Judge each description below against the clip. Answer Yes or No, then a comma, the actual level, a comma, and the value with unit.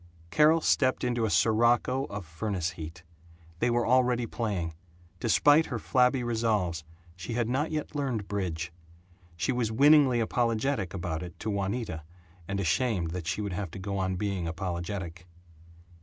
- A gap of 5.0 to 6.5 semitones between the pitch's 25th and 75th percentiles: Yes, wide, 5.5 semitones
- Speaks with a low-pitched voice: Yes, low, 105 Hz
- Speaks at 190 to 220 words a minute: No, average, 155 wpm